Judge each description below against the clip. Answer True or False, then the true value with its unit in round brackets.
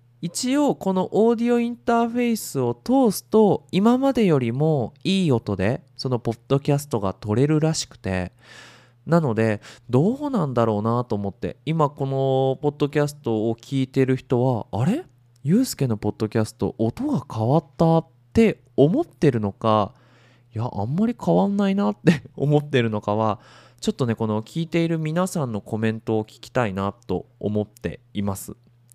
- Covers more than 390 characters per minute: False (340 characters per minute)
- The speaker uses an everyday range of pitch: False (6.6 semitones)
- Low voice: True (130 Hz)